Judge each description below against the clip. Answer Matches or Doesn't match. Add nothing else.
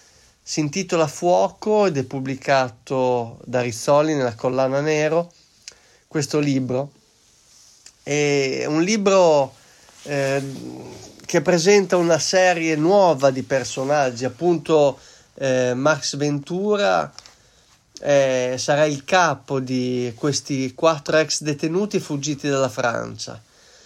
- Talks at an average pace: Doesn't match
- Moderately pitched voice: Matches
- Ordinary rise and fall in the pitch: Matches